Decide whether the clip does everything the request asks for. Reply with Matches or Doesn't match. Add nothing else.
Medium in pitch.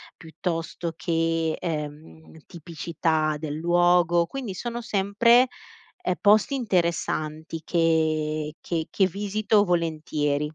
Matches